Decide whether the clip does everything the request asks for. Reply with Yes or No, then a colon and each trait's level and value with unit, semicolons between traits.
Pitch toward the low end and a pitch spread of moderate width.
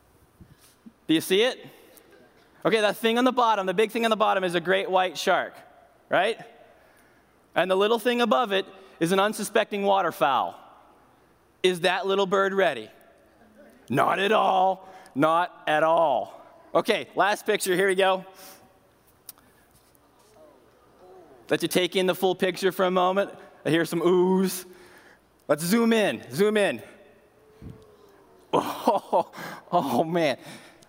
No: high, 190 Hz; average, 3.2 semitones